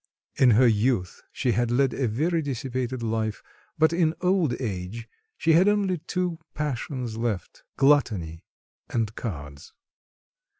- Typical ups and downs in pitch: No, wide, 6.0 semitones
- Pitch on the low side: Yes, low, 125 Hz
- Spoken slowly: Yes, slow, 130 wpm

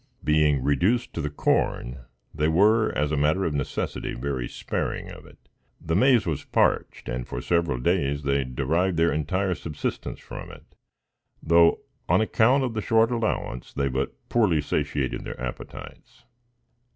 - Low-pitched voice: Yes, very low, 80 Hz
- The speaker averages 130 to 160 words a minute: Yes, average, 155 wpm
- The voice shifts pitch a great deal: Yes, wide, 5.7 semitones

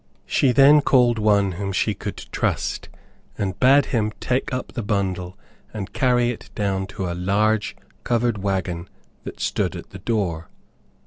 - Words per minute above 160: No, average, 155 wpm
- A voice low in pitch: Yes, low, 105 Hz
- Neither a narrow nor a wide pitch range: Yes, average, 4.2 semitones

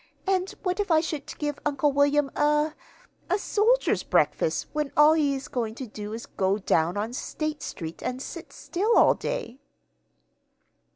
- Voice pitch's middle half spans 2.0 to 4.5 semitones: No, average, 5.3 semitones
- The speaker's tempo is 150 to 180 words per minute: Yes, average, 170 wpm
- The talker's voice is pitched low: No, very high, 295 Hz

